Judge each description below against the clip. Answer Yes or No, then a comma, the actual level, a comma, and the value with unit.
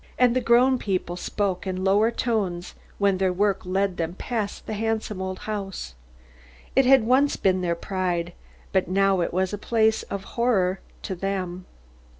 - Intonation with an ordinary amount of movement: Yes, average, 3.1 semitones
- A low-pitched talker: No, high, 195 Hz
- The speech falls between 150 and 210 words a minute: Yes, average, 165 wpm